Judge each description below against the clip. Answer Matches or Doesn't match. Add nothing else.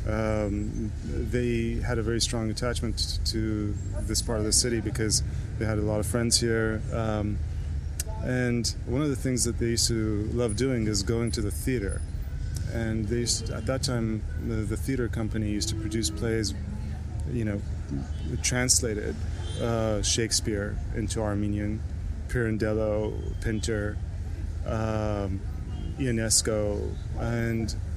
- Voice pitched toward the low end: Matches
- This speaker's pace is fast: Doesn't match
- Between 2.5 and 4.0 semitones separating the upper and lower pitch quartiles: Matches